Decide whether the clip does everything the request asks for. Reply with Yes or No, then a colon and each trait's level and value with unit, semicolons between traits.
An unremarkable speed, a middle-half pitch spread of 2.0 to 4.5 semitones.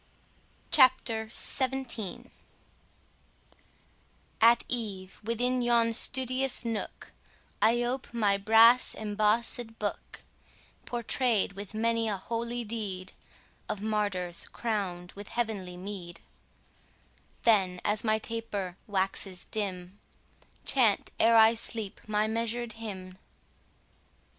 No: slow, 100 wpm; average, 2.9 semitones